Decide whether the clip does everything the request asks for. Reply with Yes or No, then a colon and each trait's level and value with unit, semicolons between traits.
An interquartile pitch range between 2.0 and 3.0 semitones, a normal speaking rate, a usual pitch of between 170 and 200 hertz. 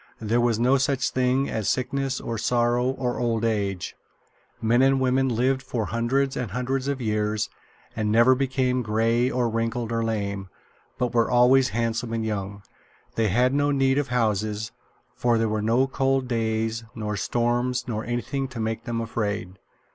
No: narrow, 2.6 semitones; average, 170 wpm; low, 120 Hz